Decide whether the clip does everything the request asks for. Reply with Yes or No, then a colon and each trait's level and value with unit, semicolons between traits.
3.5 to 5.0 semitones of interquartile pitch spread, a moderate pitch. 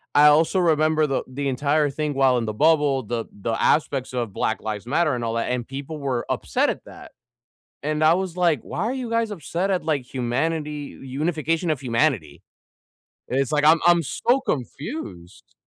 Yes: average, 4.4 semitones; medium, 145 Hz